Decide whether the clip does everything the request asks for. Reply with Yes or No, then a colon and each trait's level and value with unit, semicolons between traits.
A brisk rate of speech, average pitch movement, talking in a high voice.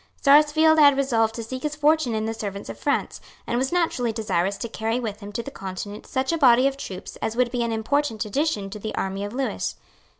Yes: fast, 230 wpm; average, 4.6 semitones; high, 235 Hz